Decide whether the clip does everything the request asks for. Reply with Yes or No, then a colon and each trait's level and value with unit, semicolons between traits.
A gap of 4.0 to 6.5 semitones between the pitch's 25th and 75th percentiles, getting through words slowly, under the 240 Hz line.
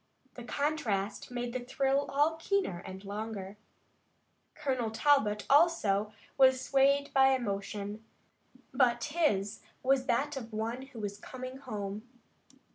No: average, 4.8 semitones; slow, 125 wpm; high, 245 Hz